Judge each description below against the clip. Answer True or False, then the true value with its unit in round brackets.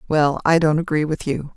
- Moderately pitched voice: True (155 Hz)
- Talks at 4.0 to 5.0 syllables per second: False (5.3 syllables/s)